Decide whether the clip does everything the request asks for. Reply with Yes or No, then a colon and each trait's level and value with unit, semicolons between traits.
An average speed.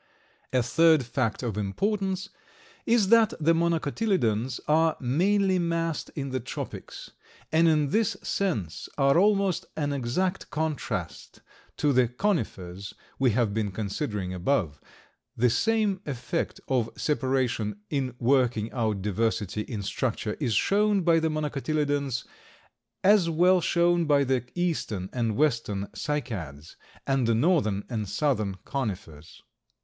No: slow, 125 wpm